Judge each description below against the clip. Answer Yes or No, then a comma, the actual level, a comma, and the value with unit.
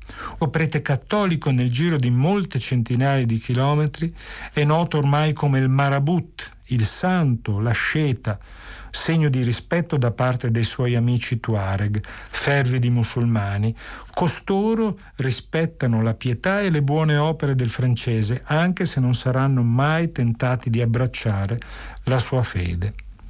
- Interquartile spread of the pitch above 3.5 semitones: Yes, average, 4.6 semitones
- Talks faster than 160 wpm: No, average, 135 wpm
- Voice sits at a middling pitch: No, low, 130 Hz